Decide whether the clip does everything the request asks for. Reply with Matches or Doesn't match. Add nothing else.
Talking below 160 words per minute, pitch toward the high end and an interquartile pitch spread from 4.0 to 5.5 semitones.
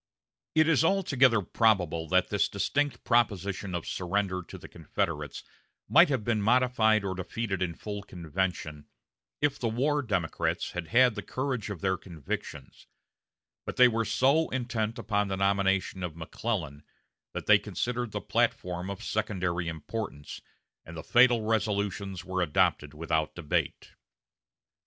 Doesn't match